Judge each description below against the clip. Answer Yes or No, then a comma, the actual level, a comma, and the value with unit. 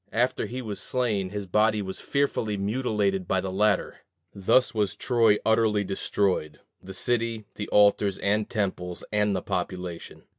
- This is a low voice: Yes, low, 105 Hz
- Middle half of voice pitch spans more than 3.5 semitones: No, narrow, 2.5 semitones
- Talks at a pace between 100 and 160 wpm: Yes, average, 150 wpm